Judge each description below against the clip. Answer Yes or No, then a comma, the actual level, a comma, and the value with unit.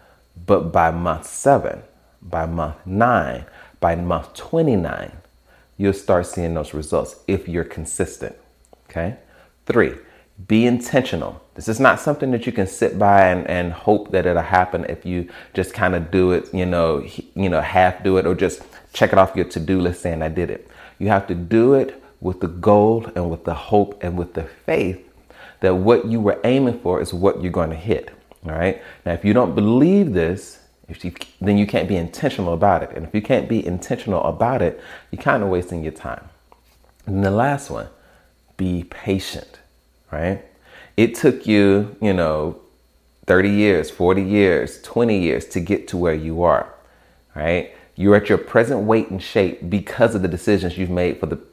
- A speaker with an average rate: Yes, average, 190 wpm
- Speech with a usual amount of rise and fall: Yes, average, 3.2 semitones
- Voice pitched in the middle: No, very low, 90 Hz